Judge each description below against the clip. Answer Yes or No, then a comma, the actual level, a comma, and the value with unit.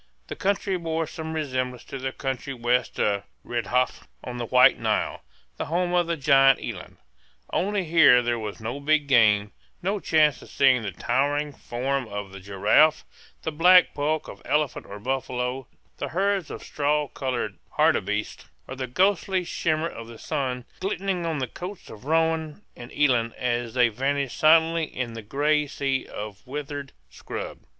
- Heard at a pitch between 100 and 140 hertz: Yes, low, 135 Hz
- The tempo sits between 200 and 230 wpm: No, average, 165 wpm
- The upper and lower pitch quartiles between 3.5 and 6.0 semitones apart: Yes, average, 4.7 semitones